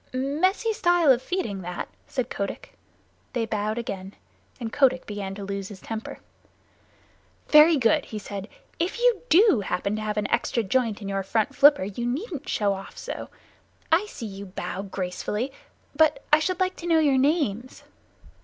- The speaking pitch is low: No, high, 235 Hz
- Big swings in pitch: Yes, wide, 7.6 semitones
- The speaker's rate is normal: Yes, average, 170 wpm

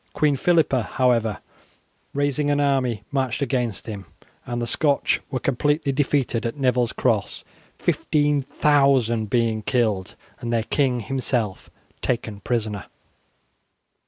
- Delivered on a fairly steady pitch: No, average, 3.5 semitones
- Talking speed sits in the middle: No, slow, 115 wpm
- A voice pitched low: Yes, low, 125 Hz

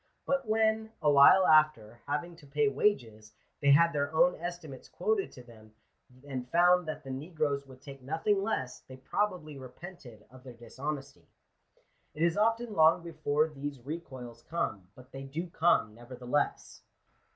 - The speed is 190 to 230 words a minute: No, average, 155 wpm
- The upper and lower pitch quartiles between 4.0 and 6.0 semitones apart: Yes, average, 4.8 semitones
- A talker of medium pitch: Yes, medium, 145 Hz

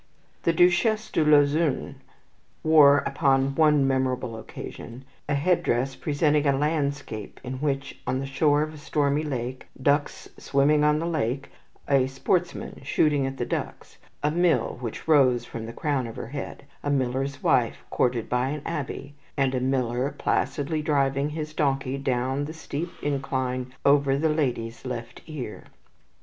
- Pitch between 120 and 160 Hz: Yes, medium, 140 Hz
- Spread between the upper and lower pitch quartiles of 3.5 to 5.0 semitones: No, narrow, 2.5 semitones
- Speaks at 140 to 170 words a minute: Yes, average, 160 wpm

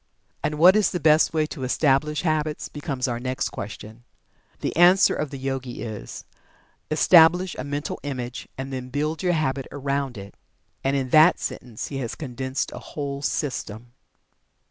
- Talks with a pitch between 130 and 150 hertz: Yes, medium, 140 Hz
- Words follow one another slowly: No, average, 165 wpm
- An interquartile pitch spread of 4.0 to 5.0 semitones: No, average, 3.2 semitones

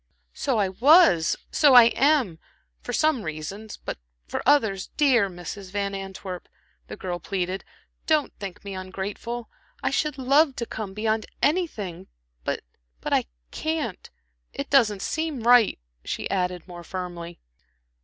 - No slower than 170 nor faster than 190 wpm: No, average, 140 wpm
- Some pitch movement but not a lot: No, wide, 6.3 semitones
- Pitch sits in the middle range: No, high, 205 Hz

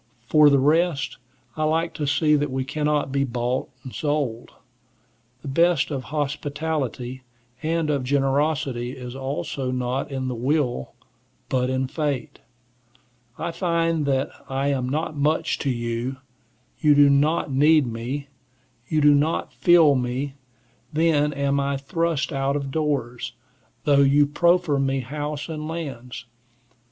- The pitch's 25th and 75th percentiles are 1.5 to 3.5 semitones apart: Yes, narrow, 2.6 semitones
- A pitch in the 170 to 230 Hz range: No, medium, 140 Hz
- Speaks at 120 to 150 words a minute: Yes, average, 140 wpm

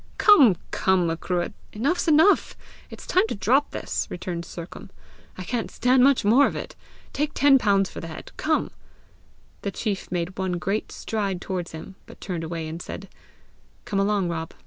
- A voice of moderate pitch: No, high, 195 Hz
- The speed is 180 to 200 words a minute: No, average, 170 wpm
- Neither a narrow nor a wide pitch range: No, wide, 6.3 semitones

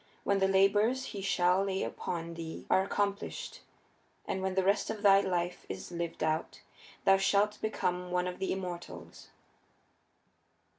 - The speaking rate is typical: Yes, average, 150 wpm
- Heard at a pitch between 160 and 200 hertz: Yes, high, 190 Hz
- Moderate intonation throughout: No, narrow, 1.9 semitones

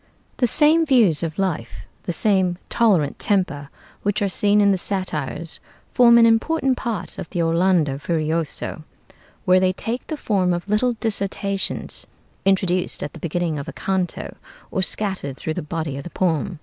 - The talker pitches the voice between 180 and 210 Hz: Yes, medium, 185 Hz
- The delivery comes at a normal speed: Yes, average, 165 wpm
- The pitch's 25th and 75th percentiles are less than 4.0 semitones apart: No, average, 4.3 semitones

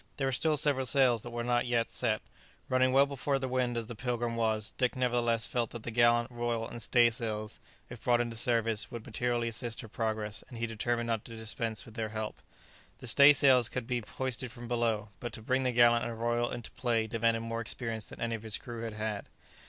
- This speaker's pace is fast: Yes, fast, 225 wpm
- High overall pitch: No, low, 120 Hz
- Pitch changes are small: Yes, narrow, 1.4 semitones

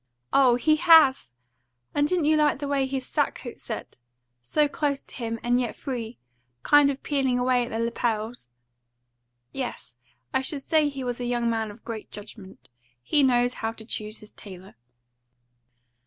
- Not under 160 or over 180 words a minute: Yes, average, 170 wpm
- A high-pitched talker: Yes, high, 245 Hz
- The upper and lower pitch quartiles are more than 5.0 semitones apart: No, average, 3.8 semitones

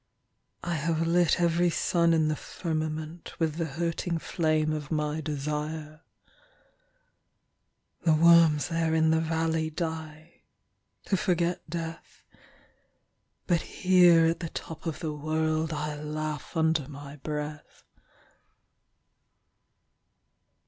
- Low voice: No, medium, 160 Hz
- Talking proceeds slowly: Yes, slow, 95 wpm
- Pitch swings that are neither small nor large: No, narrow, 1.6 semitones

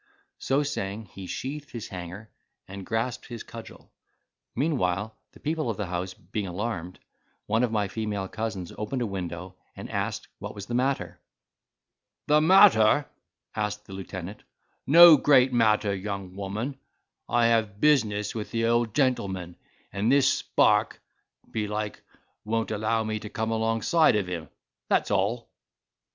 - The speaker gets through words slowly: No, average, 145 wpm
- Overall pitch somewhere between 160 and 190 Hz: No, low, 110 Hz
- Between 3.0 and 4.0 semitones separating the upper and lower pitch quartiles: Yes, average, 3.6 semitones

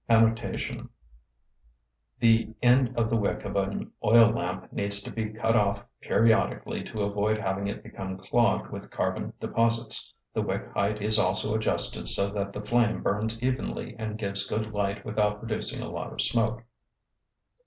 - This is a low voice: Yes, low, 105 Hz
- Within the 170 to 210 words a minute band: No, average, 155 wpm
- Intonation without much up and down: Yes, narrow, 2.1 semitones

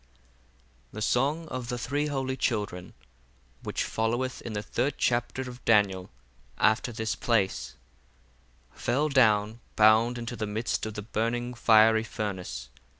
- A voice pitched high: No, low, 115 Hz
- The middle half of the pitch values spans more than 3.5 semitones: No, average, 2.8 semitones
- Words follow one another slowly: Yes, slow, 130 wpm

